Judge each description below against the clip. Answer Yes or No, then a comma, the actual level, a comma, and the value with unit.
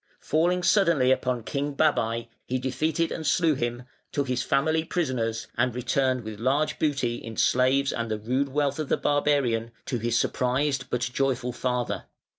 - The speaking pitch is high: No, low, 130 Hz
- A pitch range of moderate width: Yes, average, 3.4 semitones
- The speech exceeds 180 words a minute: No, average, 165 wpm